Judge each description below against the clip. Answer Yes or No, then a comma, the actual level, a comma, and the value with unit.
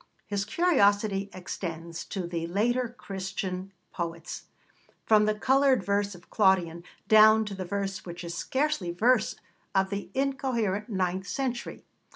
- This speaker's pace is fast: No, slow, 135 wpm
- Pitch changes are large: No, average, 3.4 semitones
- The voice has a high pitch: Yes, high, 200 Hz